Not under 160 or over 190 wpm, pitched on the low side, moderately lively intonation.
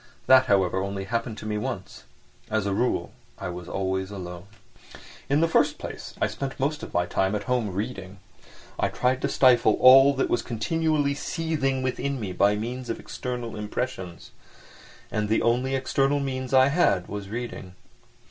Yes: average, 170 wpm; low, 120 Hz; average, 5.0 semitones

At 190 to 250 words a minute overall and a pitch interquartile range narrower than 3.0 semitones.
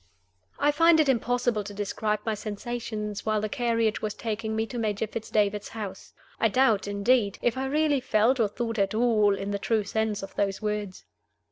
Yes: average, 195 wpm; narrow, 2.6 semitones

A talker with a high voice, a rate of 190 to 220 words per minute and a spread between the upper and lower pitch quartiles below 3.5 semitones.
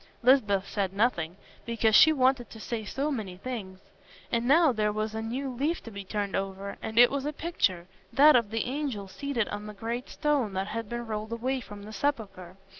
No: high, 225 Hz; average, 200 wpm; average, 4.4 semitones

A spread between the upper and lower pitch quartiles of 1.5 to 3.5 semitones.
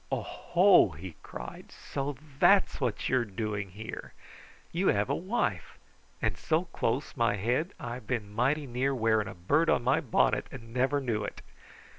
No: average, 5.3 semitones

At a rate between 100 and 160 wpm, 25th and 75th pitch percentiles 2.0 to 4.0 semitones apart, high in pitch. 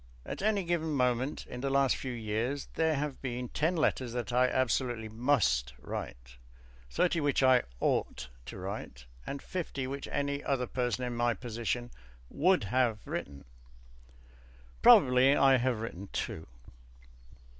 No: average, 145 wpm; average, 3.5 semitones; low, 125 Hz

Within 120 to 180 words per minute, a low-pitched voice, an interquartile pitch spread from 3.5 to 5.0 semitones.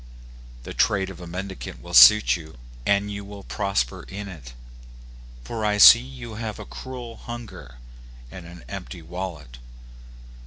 Yes: average, 150 wpm; very low, 95 Hz; average, 4.3 semitones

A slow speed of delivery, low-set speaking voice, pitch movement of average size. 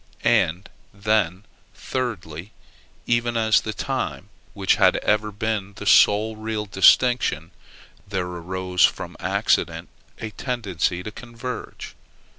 Yes: slow, 115 wpm; low, 105 Hz; average, 3.4 semitones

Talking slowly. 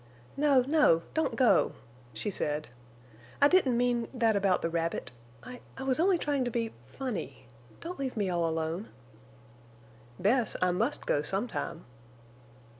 Yes: slow, 130 wpm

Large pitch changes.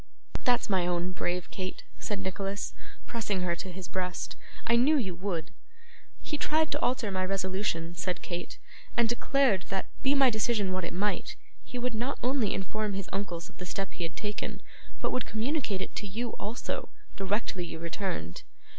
No: average, 4.3 semitones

